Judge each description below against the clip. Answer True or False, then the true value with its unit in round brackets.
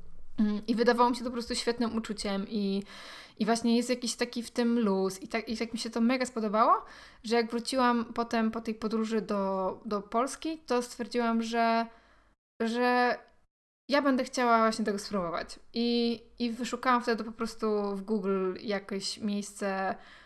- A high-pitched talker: True (230 Hz)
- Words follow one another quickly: True (170 wpm)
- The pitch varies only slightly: True (1.9 semitones)